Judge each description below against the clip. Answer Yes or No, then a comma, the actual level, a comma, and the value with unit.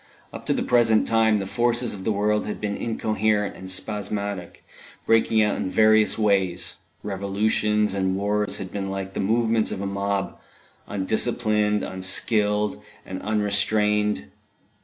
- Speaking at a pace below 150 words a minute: Yes, average, 140 wpm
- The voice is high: No, low, 105 Hz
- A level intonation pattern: Yes, narrow, 1.8 semitones